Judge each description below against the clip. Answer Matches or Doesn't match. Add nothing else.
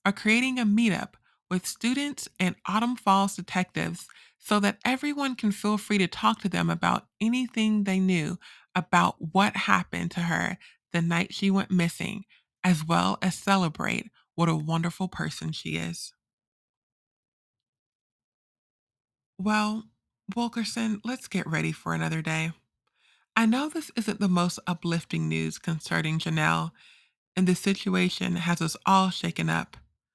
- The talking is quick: Doesn't match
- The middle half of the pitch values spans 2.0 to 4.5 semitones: Doesn't match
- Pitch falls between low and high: Matches